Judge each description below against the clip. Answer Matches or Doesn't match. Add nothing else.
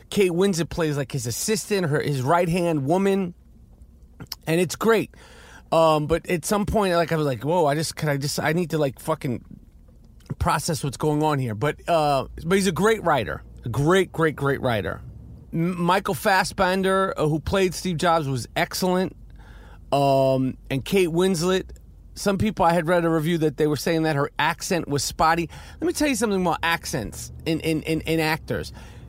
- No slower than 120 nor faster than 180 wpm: Doesn't match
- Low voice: Doesn't match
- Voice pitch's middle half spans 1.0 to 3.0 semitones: Doesn't match